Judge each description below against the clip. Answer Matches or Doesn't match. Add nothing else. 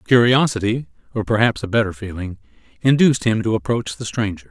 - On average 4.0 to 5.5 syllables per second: Doesn't match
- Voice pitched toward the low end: Matches